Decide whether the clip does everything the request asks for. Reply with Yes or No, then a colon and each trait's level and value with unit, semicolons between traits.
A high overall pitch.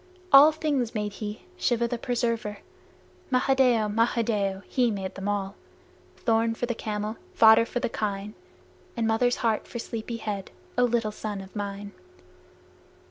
Yes: high, 225 Hz